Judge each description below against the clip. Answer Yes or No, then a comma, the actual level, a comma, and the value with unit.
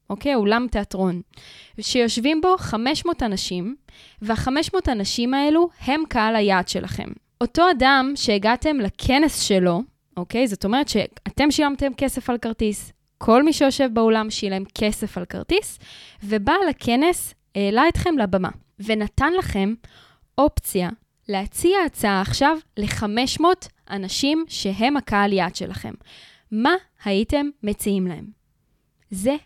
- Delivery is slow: No, average, 115 wpm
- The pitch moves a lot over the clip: Yes, wide, 5.9 semitones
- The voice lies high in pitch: Yes, high, 235 Hz